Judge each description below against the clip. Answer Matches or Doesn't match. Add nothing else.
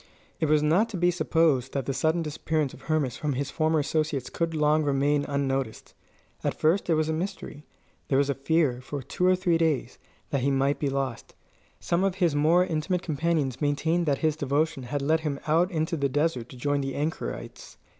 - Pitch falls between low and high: Matches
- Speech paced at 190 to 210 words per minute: Matches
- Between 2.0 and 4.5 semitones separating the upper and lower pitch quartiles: Matches